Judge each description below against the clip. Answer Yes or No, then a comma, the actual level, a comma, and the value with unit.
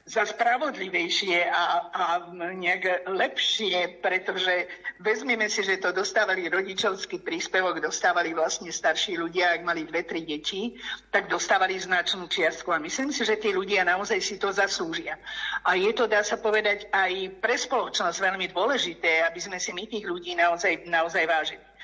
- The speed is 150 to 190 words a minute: Yes, average, 155 wpm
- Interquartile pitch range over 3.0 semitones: Yes, average, 3.4 semitones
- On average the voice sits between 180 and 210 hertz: Yes, medium, 185 Hz